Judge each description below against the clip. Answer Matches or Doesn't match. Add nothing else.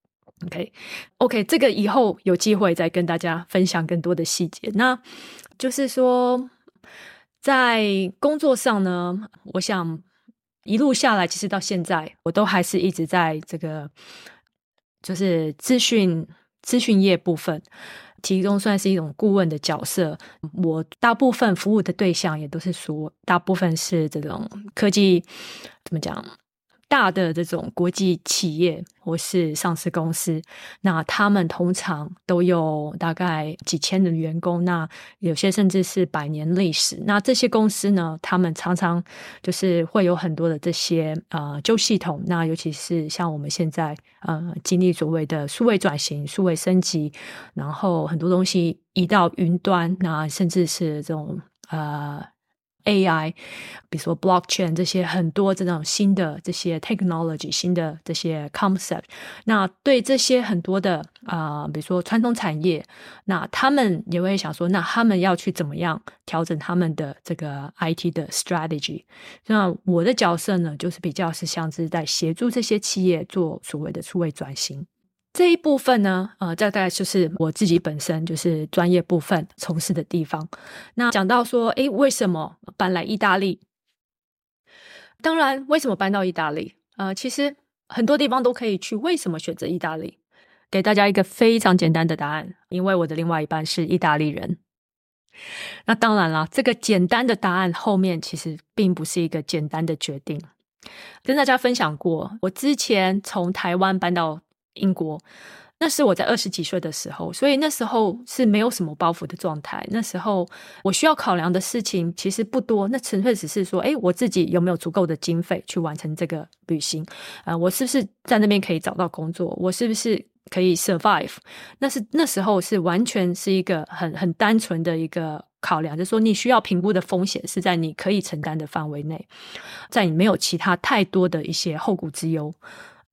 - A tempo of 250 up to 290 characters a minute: Matches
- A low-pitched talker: Doesn't match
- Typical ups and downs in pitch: Matches